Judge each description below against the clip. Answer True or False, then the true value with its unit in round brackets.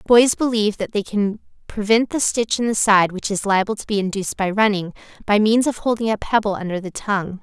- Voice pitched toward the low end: False (210 Hz)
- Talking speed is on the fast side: True (225 wpm)